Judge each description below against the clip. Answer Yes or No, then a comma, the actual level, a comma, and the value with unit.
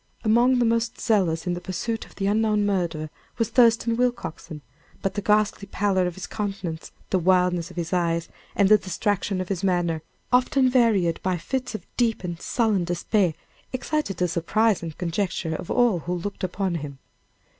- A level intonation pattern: No, average, 4.3 semitones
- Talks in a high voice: Yes, high, 195 Hz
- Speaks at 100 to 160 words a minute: No, average, 175 wpm